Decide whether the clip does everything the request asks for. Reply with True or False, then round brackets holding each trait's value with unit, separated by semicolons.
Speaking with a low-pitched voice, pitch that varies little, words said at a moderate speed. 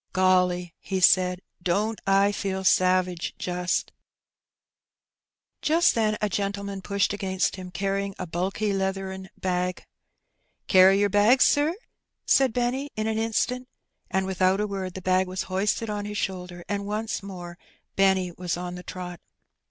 False (190 Hz; 2.0 semitones; 155 wpm)